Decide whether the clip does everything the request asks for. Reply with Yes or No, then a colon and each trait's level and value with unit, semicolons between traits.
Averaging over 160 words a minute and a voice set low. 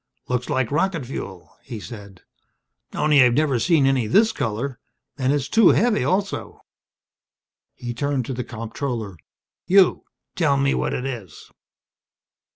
No: average, 140 wpm; low, 130 Hz